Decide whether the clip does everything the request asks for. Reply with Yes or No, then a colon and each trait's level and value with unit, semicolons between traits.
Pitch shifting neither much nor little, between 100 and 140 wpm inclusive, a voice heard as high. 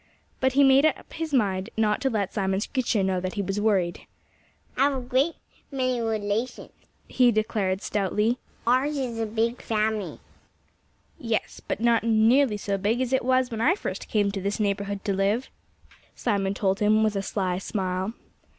No: average, 4.0 semitones; average, 180 wpm; high, 220 Hz